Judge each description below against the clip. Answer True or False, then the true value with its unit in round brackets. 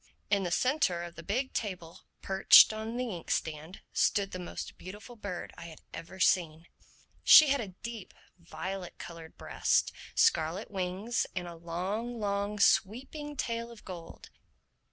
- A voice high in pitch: True (195 Hz)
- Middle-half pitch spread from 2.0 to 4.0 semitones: False (4.7 semitones)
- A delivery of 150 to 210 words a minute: True (155 wpm)